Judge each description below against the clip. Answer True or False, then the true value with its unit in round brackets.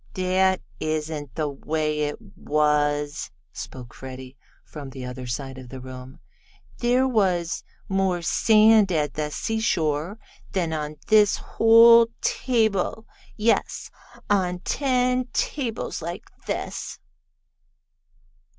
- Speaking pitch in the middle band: True (165 Hz)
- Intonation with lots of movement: True (6.7 semitones)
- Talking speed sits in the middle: False (105 wpm)